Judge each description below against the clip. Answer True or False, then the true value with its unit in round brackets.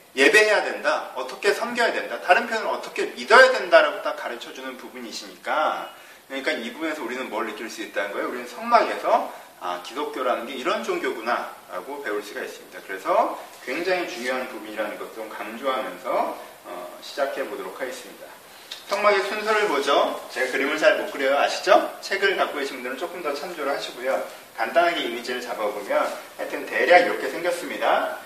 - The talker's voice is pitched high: True (215 Hz)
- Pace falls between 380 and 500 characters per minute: True (405 characters per minute)